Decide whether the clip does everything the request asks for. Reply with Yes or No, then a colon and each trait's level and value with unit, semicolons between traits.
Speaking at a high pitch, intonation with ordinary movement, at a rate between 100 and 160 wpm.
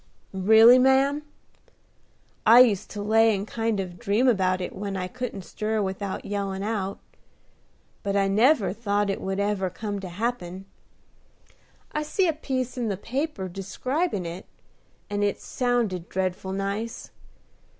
Yes: high, 205 Hz; average, 3.8 semitones; average, 145 wpm